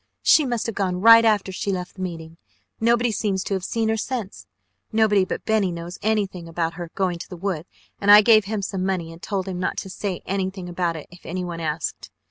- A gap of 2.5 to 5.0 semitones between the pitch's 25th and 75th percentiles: Yes, average, 3.2 semitones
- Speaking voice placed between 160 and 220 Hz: Yes, high, 190 Hz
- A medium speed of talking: No, fast, 225 wpm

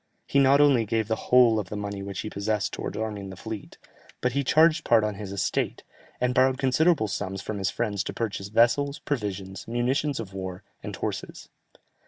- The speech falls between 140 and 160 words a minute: No, average, 195 wpm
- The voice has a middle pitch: No, low, 110 Hz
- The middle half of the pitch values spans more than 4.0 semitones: Yes, average, 4.4 semitones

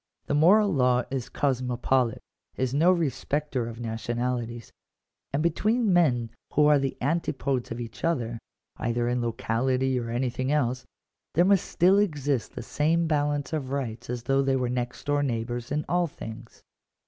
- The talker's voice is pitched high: No, low, 130 Hz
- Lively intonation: No, average, 3.7 semitones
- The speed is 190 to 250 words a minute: No, average, 160 wpm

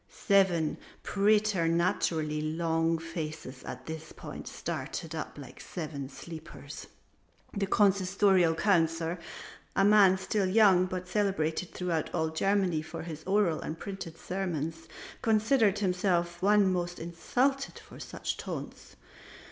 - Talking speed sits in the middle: No, slow, 125 wpm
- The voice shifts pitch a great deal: No, average, 3.4 semitones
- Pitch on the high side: No, medium, 175 Hz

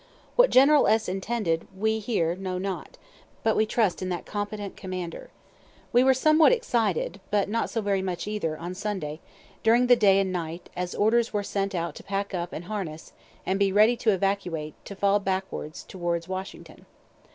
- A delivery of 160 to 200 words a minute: Yes, average, 180 wpm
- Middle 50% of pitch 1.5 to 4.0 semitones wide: Yes, average, 3.2 semitones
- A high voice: Yes, high, 195 Hz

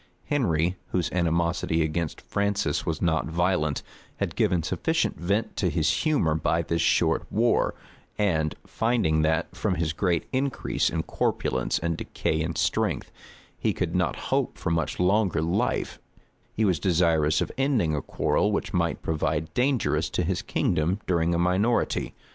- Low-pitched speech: Yes, very low, 85 Hz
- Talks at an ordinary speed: Yes, average, 155 wpm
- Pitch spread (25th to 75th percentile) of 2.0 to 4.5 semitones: Yes, average, 3.6 semitones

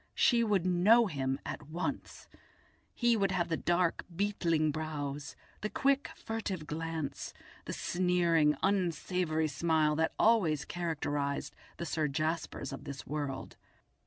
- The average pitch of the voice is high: No, medium, 165 Hz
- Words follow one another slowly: Yes, slow, 130 wpm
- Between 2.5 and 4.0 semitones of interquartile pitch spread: Yes, average, 3.6 semitones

